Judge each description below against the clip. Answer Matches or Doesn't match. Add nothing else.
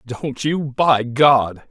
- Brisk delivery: Doesn't match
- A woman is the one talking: Doesn't match